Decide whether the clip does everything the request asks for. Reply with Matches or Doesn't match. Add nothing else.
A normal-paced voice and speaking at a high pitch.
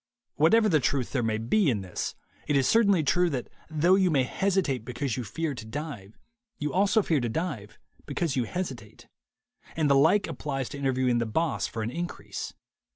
Doesn't match